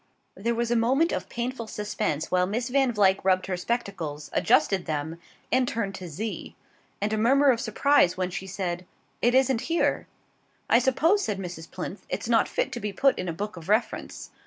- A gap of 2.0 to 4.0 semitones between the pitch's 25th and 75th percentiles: No, average, 5.1 semitones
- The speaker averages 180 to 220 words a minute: Yes, average, 195 wpm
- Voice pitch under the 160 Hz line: No, high, 210 Hz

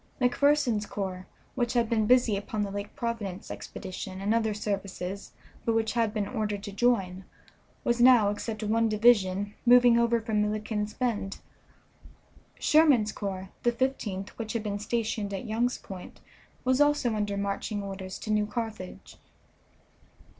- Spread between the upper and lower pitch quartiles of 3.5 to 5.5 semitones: No, average, 2.9 semitones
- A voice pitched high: Yes, high, 215 Hz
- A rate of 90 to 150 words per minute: Yes, average, 145 wpm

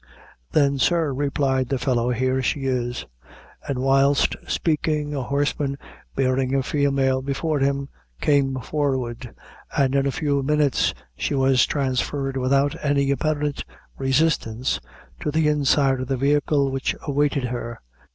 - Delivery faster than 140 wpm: No, slow, 135 wpm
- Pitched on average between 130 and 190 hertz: Yes, low, 135 Hz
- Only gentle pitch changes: Yes, narrow, 1.7 semitones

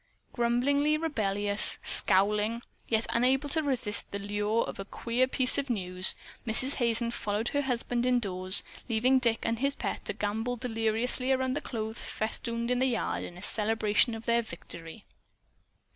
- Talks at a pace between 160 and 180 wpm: No, average, 145 wpm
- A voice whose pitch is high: Yes, high, 230 Hz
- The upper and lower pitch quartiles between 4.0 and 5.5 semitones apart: No, average, 3.2 semitones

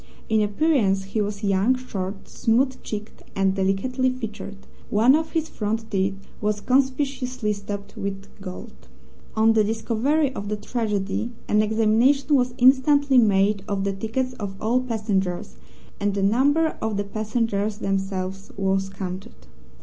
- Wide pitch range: No, average, 4.3 semitones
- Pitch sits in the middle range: No, high, 215 Hz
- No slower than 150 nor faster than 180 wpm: No, average, 140 wpm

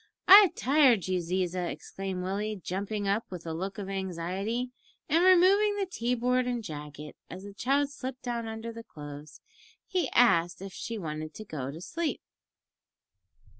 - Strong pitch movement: Yes, wide, 5.8 semitones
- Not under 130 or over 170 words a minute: Yes, average, 165 wpm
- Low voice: No, high, 205 Hz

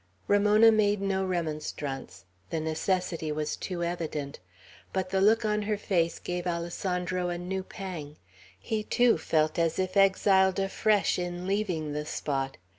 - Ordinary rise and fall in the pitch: Yes, average, 3.6 semitones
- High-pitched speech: No, medium, 180 Hz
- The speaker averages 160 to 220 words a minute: No, average, 145 wpm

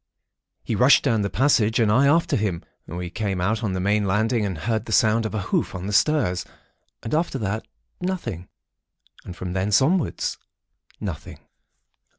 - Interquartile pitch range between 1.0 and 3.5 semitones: No, average, 4.2 semitones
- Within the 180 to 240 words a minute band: No, average, 170 wpm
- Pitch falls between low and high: No, low, 110 Hz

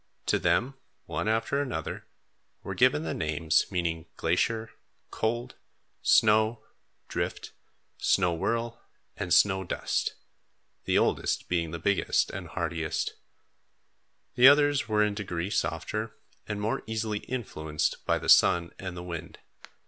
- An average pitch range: Yes, average, 5.0 semitones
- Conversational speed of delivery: No, slow, 125 wpm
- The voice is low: Yes, low, 100 Hz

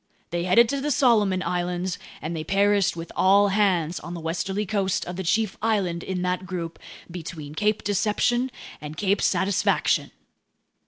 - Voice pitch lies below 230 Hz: Yes, high, 190 Hz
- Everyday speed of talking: Yes, average, 160 wpm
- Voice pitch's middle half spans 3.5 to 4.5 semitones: No, average, 3.1 semitones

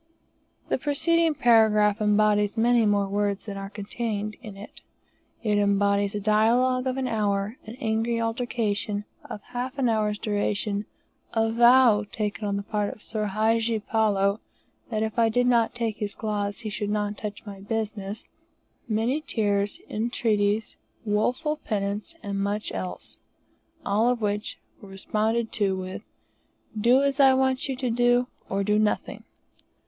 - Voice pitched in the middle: No, high, 215 Hz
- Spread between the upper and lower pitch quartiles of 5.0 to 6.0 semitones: No, narrow, 2.4 semitones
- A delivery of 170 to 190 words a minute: No, average, 155 wpm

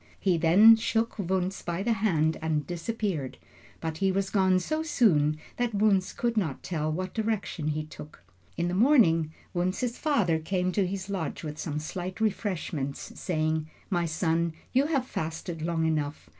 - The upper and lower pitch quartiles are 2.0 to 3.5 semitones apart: No, average, 4.6 semitones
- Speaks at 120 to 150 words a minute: No, average, 165 wpm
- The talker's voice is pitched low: No, medium, 180 Hz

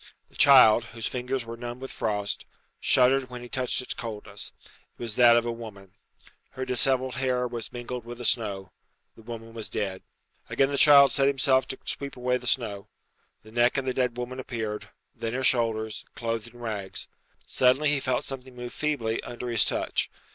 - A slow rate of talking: No, average, 190 wpm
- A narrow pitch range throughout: Yes, narrow, 2.3 semitones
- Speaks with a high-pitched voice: No, low, 120 Hz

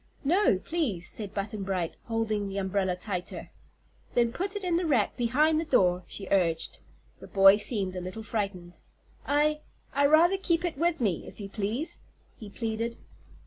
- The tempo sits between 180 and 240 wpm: No, average, 170 wpm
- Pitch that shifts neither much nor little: No, wide, 7.7 semitones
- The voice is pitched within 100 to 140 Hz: No, high, 220 Hz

